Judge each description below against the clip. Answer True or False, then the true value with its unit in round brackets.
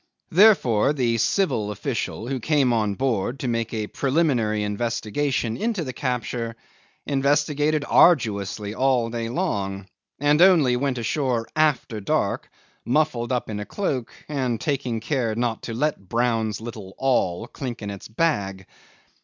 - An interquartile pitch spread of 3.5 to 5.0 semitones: True (4.3 semitones)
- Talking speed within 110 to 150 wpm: True (145 wpm)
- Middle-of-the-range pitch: False (120 Hz)